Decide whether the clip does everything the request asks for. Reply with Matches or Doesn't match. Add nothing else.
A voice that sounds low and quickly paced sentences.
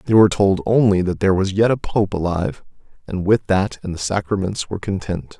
Matches